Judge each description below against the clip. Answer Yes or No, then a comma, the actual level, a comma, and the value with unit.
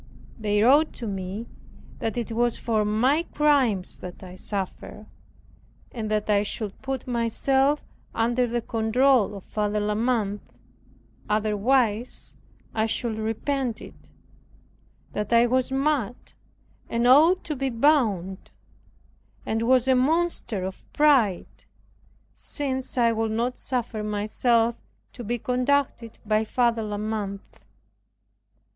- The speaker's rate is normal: No, slow, 125 wpm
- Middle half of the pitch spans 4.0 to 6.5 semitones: No, average, 3.5 semitones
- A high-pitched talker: Yes, high, 230 Hz